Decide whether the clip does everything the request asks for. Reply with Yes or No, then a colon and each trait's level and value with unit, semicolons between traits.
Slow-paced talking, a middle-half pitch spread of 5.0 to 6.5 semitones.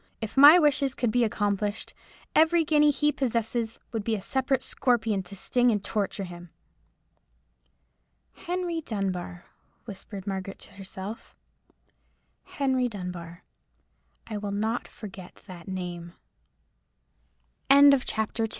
Yes: slow, 115 wpm; average, 5.3 semitones